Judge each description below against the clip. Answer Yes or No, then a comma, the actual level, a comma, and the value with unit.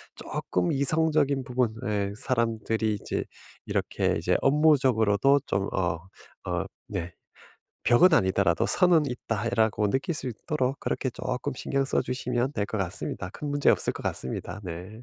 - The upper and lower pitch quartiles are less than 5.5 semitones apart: Yes, average, 5.1 semitones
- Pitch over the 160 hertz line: No, low, 120 Hz